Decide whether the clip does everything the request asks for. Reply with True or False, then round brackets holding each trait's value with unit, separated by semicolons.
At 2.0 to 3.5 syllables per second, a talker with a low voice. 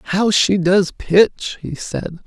False (3.1 syllables/s; 185 Hz)